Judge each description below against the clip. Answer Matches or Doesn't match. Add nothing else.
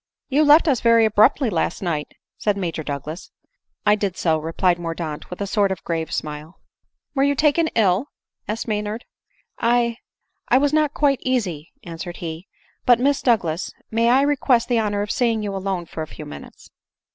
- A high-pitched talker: Matches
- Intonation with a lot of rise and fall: Matches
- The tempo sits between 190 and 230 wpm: Matches